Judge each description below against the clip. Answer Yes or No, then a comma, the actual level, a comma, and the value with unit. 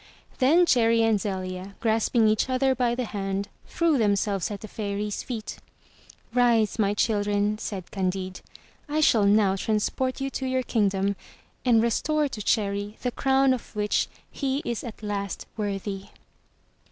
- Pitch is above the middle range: Yes, high, 215 Hz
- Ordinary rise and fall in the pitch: Yes, average, 3.7 semitones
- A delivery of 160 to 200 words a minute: No, average, 150 wpm